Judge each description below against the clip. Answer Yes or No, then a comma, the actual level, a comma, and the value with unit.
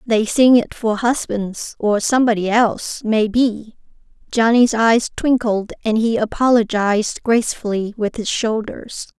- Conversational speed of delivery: No, slow, 125 wpm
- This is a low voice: No, high, 225 Hz